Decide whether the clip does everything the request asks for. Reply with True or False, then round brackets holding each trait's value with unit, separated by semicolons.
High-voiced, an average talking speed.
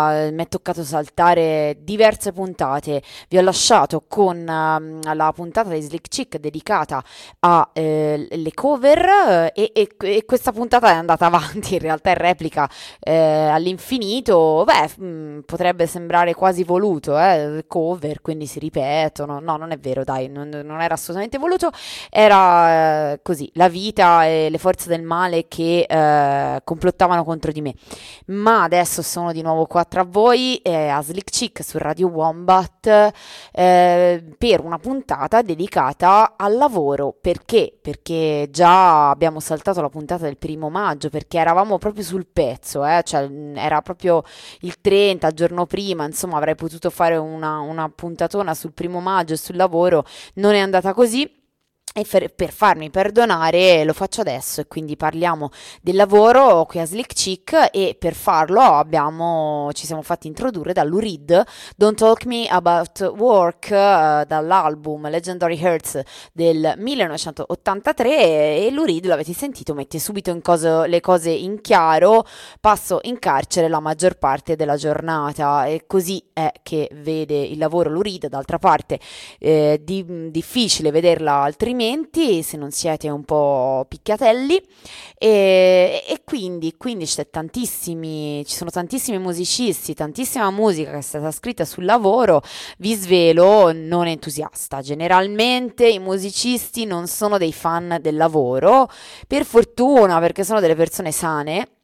False (170 Hz; 150 wpm)